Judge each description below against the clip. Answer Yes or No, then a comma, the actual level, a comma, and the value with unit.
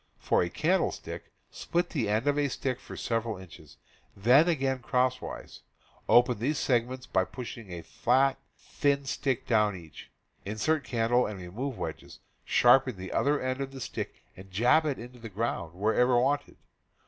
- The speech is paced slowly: No, average, 160 wpm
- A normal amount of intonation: Yes, average, 4.1 semitones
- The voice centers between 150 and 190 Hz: No, low, 125 Hz